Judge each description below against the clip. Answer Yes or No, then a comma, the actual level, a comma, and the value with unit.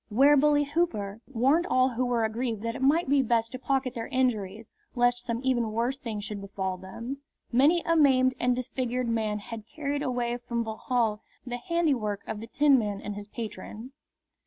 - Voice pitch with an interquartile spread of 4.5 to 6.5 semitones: No, average, 3.3 semitones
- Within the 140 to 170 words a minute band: No, average, 185 wpm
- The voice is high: Yes, high, 245 Hz